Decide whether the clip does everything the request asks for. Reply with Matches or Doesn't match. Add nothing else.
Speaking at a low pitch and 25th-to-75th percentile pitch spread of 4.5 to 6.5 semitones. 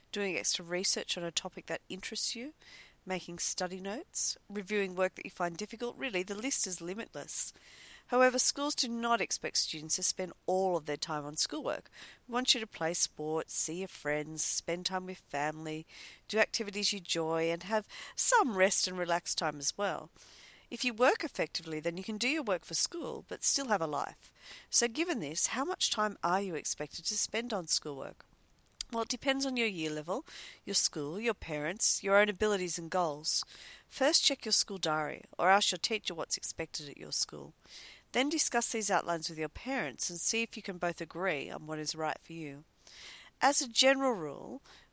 Doesn't match